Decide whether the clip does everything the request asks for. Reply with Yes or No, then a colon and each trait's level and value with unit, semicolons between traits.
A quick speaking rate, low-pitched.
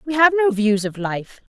No: fast, 230 wpm; high, 245 Hz